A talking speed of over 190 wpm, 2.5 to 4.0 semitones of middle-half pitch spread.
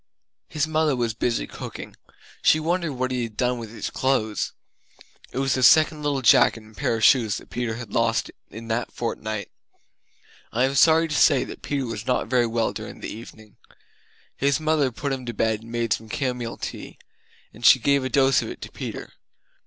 Yes: average, 200 wpm; average, 3.5 semitones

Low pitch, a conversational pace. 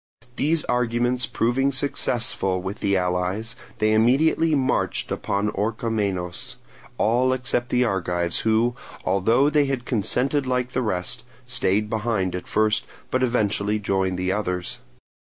No: low, 110 Hz; slow, 130 wpm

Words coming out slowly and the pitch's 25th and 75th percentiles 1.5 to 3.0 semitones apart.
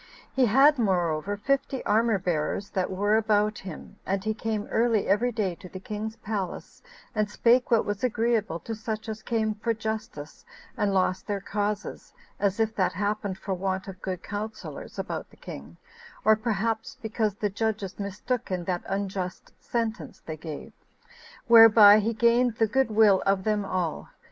No: average, 170 wpm; average, 2.7 semitones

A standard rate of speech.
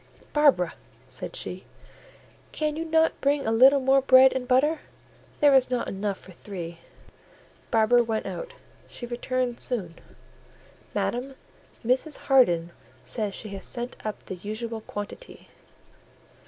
No: slow, 130 wpm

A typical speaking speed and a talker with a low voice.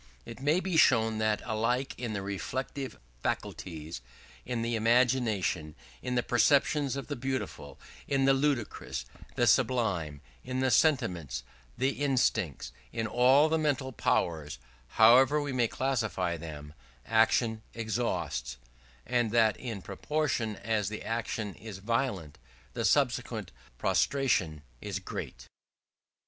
No: slow, 125 wpm; low, 115 Hz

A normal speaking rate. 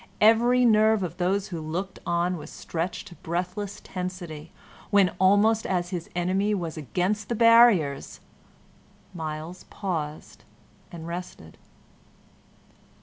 No: slow, 115 wpm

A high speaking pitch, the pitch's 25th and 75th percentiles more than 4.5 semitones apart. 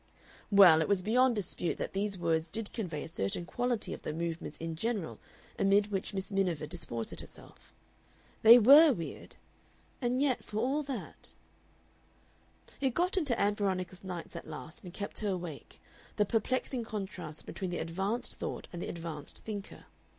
Yes: high, 195 Hz; average, 5.2 semitones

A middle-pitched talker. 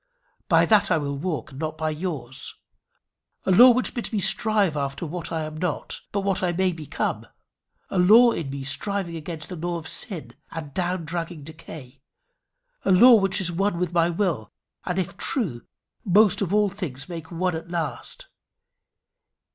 Yes: medium, 170 Hz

